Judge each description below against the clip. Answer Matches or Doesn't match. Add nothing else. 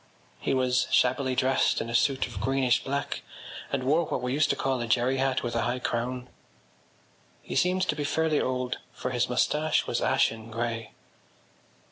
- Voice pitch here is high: Doesn't match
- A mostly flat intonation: Matches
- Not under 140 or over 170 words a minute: Doesn't match